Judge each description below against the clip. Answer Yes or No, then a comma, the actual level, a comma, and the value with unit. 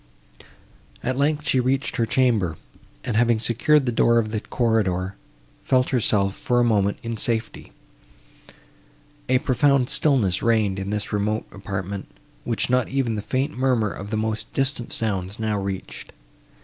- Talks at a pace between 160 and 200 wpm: No, average, 150 wpm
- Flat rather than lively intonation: No, average, 3.9 semitones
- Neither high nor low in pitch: No, low, 115 Hz